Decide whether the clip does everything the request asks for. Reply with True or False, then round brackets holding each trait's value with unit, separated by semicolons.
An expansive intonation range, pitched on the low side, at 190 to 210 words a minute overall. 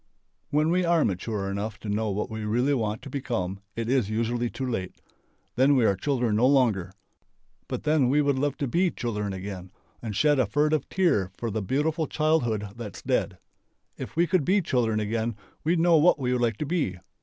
True (5.8 semitones; 120 Hz; 200 wpm)